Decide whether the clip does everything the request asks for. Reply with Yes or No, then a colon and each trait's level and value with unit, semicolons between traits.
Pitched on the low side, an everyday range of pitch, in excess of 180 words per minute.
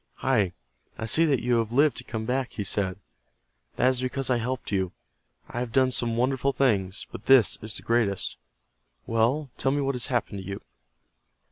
Yes: low, 120 Hz; average, 3.6 semitones; average, 195 wpm